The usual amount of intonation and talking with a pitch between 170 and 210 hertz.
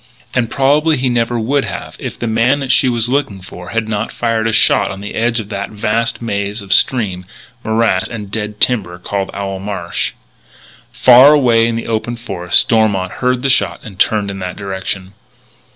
No: average, 3.3 semitones; low, 110 Hz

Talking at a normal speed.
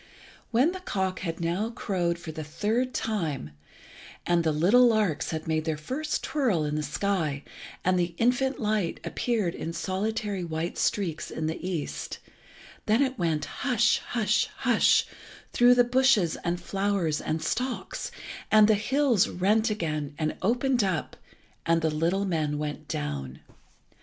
Yes: average, 150 wpm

